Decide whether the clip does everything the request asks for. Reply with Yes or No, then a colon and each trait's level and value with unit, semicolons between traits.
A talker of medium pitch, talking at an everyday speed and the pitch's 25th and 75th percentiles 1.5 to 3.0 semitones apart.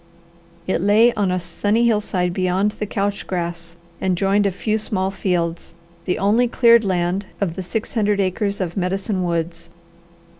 No: high, 195 Hz; average, 160 wpm; narrow, 2.6 semitones